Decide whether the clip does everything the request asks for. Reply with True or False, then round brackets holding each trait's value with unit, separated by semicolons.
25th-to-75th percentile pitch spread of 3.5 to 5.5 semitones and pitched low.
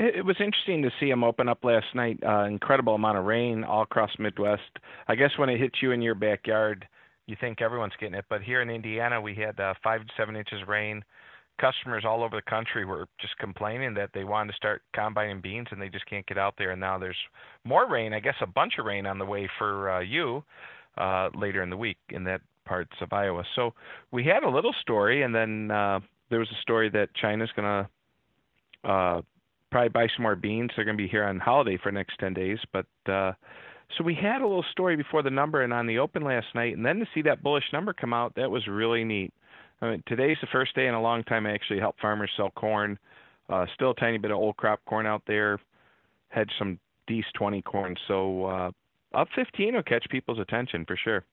False (3.0 semitones; 110 Hz)